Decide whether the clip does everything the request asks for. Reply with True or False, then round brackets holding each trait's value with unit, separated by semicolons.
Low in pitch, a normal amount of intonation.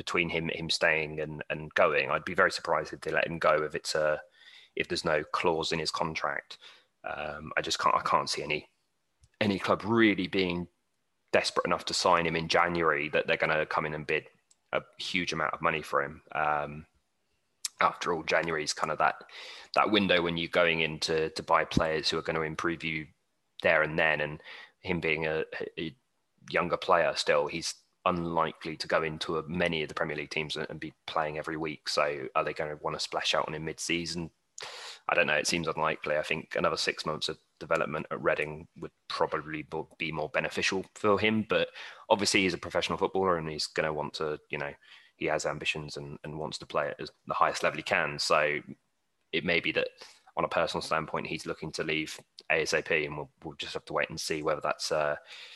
False (80 Hz; 2.1 semitones)